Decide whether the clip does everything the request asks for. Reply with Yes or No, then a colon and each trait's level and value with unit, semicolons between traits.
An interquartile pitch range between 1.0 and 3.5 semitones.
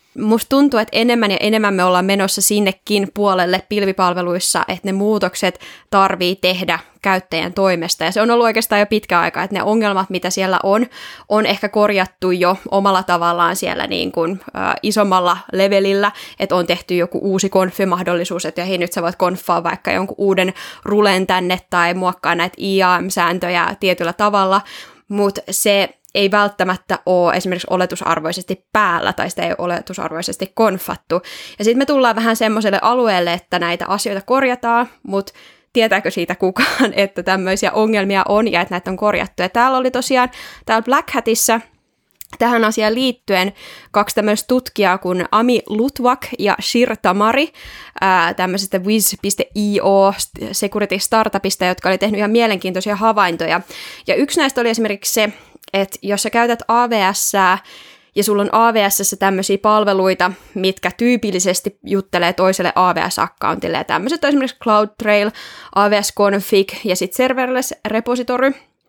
Yes: average, 3.0 semitones